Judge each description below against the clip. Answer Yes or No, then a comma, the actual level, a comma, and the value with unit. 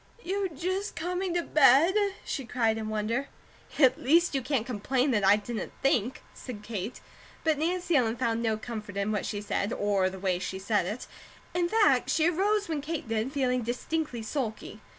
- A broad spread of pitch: Yes, wide, 6.8 semitones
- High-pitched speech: Yes, very high, 250 Hz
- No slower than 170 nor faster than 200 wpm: Yes, average, 185 wpm